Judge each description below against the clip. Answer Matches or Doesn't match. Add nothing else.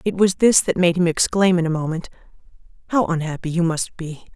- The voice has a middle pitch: Matches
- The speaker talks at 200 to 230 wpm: Matches